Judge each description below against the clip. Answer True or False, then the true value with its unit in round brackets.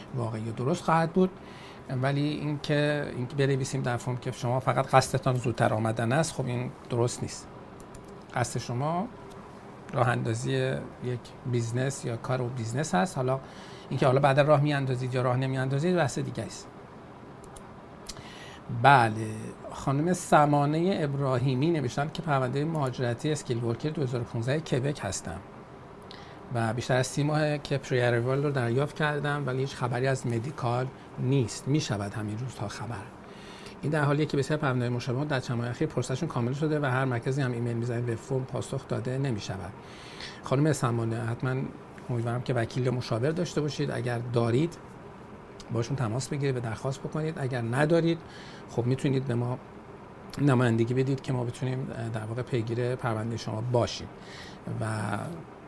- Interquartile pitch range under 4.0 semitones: True (3.2 semitones)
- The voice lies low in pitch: True (130 Hz)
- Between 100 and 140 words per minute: False (155 wpm)